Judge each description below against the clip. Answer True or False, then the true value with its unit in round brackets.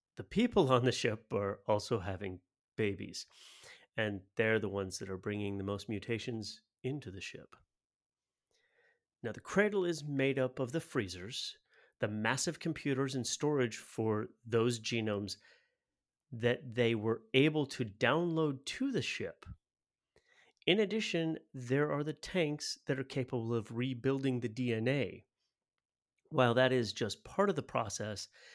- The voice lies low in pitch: True (125 Hz)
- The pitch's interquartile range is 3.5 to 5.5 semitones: True (4.7 semitones)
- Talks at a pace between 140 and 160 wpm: True (145 wpm)